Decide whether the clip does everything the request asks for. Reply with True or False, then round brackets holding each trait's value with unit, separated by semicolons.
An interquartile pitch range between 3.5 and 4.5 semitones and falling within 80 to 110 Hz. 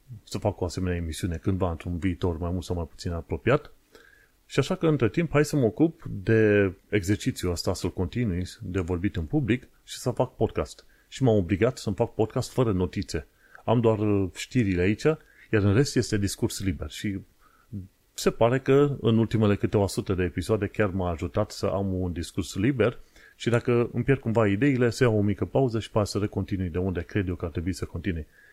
True (4.2 semitones; 105 Hz)